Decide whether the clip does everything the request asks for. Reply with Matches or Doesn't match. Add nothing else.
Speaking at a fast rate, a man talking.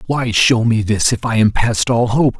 Matches